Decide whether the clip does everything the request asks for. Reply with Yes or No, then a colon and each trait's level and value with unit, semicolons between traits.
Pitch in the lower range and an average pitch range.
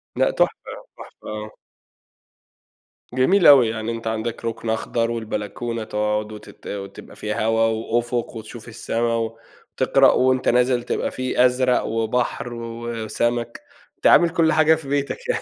No: low, 115 Hz; narrow, 2.1 semitones